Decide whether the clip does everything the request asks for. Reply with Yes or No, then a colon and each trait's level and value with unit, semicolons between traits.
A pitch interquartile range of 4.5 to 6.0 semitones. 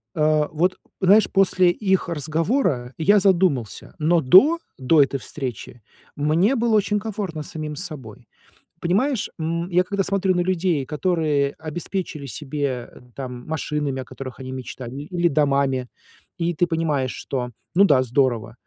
Yes: average, 5.3 semitones